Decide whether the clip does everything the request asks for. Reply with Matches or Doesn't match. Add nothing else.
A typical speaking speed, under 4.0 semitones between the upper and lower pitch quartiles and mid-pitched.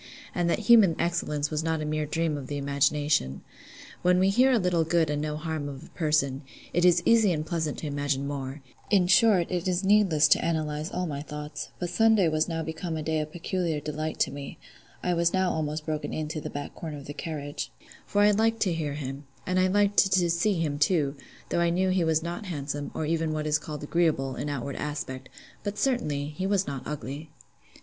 Doesn't match